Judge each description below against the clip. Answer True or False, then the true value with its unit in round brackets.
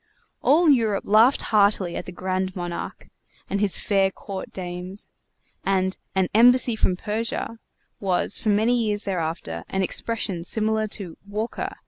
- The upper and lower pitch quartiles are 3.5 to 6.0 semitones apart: False (2.9 semitones)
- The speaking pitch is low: False (200 Hz)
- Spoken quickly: False (140 wpm)